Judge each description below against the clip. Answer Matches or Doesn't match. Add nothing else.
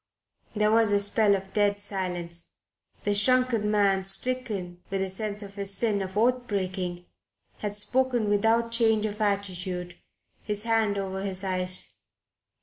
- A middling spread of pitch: Doesn't match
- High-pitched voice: Matches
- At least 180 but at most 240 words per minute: Doesn't match